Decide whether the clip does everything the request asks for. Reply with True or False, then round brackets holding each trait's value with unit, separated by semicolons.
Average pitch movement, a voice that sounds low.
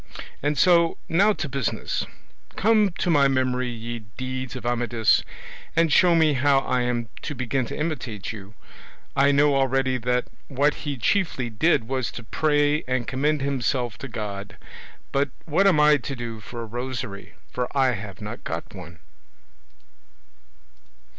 True (3.8 semitones; 130 Hz)